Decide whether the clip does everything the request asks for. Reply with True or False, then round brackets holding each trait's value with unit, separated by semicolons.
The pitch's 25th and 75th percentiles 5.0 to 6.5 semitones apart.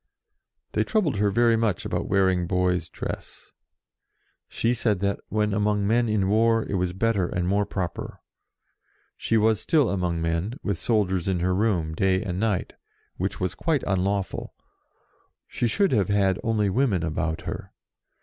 False (3.5 semitones)